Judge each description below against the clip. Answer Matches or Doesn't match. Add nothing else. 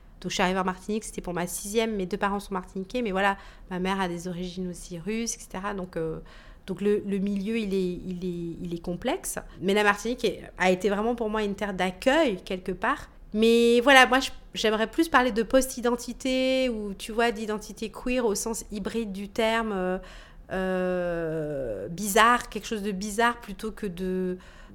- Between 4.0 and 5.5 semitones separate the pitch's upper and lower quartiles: Doesn't match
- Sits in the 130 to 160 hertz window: Doesn't match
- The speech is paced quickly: Doesn't match